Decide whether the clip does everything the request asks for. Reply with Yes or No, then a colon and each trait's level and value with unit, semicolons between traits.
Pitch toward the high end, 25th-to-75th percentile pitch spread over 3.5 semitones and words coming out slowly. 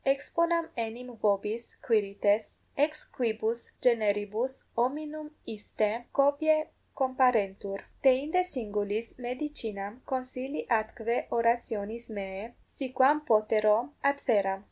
Yes: high, 235 Hz; average, 4.2 semitones; slow, 90 wpm